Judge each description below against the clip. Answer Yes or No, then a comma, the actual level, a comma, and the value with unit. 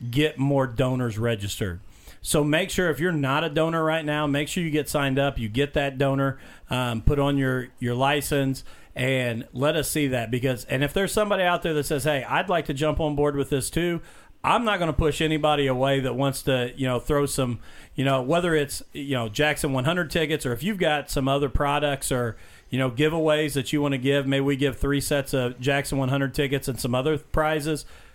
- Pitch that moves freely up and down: No, narrow, 2.6 semitones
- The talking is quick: Yes, fast, 225 wpm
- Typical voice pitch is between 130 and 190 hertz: Yes, medium, 140 Hz